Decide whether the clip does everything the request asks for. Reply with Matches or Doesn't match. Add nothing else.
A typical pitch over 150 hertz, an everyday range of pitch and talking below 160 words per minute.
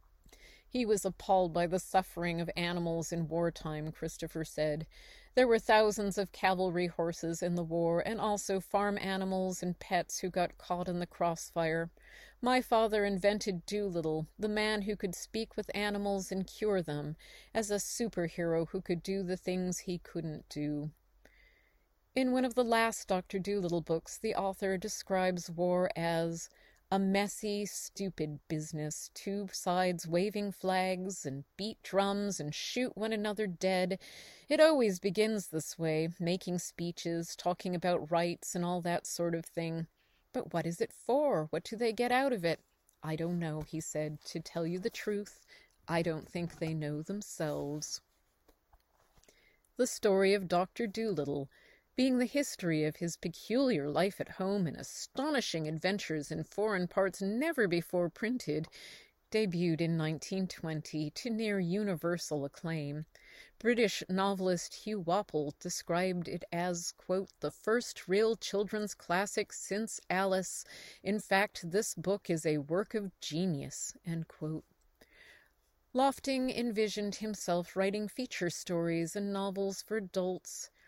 Matches